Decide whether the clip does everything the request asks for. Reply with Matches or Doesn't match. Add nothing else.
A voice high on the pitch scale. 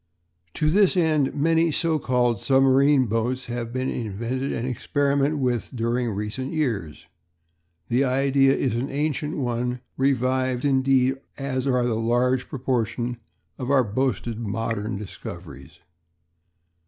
Doesn't match